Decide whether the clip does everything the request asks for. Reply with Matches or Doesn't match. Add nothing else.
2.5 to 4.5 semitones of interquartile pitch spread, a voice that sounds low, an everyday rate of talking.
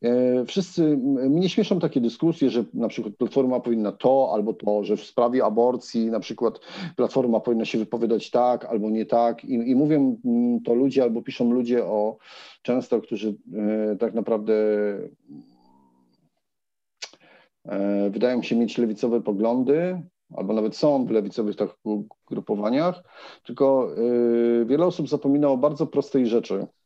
Matches